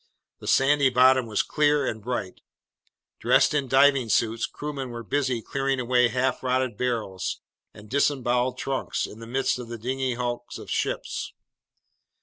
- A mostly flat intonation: Yes, narrow, 2.3 semitones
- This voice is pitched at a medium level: No, low, 125 Hz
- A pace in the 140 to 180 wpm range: Yes, average, 150 wpm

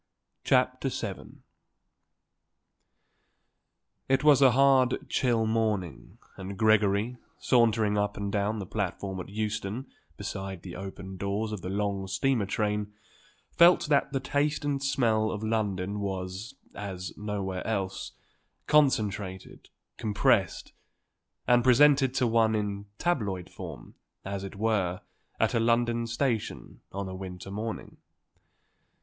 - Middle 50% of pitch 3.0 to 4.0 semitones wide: Yes, average, 3.6 semitones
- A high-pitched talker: No, low, 105 Hz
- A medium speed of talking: No, slow, 120 wpm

